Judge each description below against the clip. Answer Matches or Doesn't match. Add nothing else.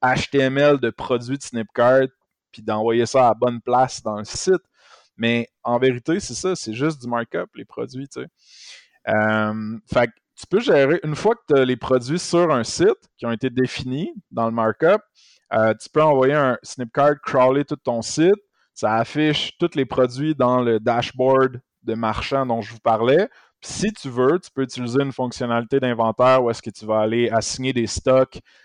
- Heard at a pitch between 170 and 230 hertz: Doesn't match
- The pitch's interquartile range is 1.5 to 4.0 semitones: Matches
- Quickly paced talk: Doesn't match